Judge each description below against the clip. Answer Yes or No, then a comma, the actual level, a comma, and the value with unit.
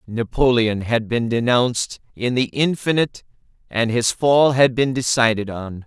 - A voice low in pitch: Yes, low, 120 Hz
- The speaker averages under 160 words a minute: Yes, average, 145 wpm